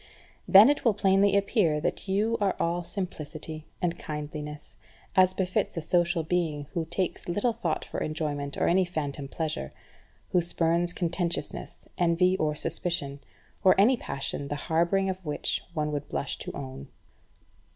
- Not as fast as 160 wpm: Yes, average, 150 wpm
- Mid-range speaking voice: Yes, medium, 170 Hz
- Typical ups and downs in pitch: Yes, average, 3.7 semitones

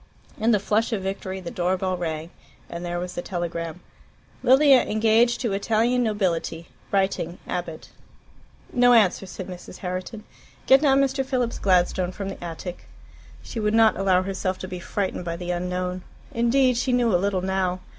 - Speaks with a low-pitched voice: No, high, 190 Hz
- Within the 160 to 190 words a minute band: Yes, average, 170 wpm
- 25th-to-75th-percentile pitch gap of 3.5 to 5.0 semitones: Yes, average, 4.2 semitones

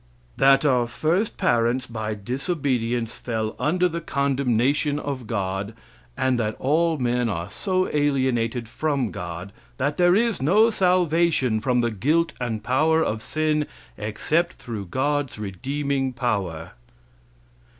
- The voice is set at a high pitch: No, low, 130 Hz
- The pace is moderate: No, slow, 130 wpm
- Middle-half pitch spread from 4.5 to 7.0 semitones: Yes, average, 5.1 semitones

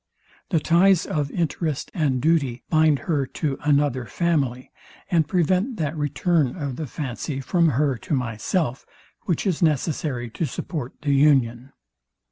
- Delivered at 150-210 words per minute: No, average, 140 wpm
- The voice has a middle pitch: Yes, medium, 150 Hz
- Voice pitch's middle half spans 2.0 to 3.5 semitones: No, average, 3.9 semitones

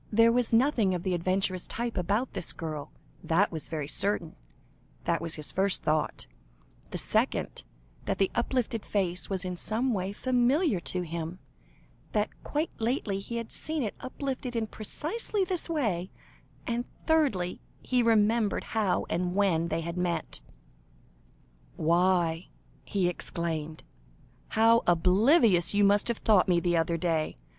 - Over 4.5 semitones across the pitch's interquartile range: Yes, average, 5.3 semitones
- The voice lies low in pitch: No, high, 195 Hz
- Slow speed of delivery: No, average, 145 wpm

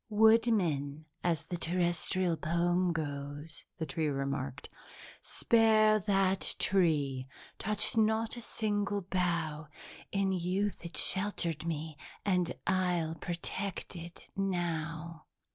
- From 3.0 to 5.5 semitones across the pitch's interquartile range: Yes, average, 3.8 semitones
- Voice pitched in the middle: Yes, medium, 175 Hz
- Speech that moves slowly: Yes, slow, 105 wpm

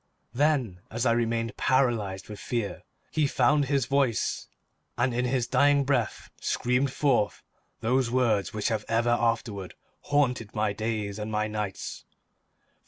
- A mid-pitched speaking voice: No, low, 120 Hz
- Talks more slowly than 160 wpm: Yes, average, 140 wpm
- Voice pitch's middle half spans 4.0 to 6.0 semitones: No, average, 3.4 semitones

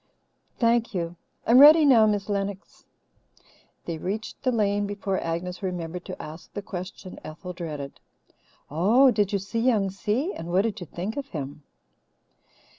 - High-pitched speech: Yes, high, 200 Hz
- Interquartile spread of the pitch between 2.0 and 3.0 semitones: No, average, 4.2 semitones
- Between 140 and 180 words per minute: Yes, average, 155 wpm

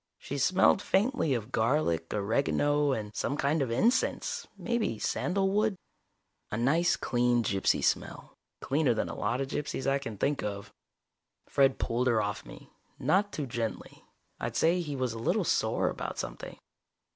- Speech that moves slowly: No, average, 155 wpm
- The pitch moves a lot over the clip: Yes, wide, 6.0 semitones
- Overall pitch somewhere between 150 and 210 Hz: No, low, 135 Hz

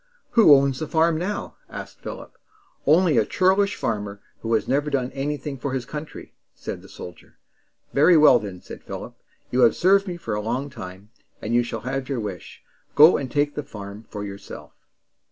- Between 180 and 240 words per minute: Yes, average, 190 wpm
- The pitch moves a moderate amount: No, wide, 5.7 semitones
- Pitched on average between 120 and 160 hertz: Yes, low, 135 Hz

